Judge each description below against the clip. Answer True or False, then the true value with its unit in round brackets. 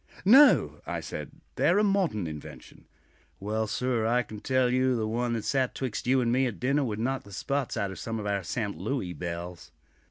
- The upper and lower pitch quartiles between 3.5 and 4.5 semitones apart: True (4.2 semitones)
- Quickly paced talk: True (215 wpm)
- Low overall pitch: True (115 Hz)